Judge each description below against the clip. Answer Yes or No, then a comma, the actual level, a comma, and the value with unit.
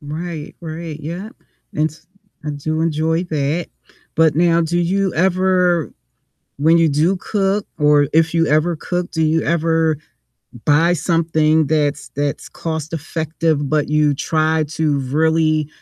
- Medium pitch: Yes, medium, 160 Hz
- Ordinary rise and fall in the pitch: No, narrow, 1.8 semitones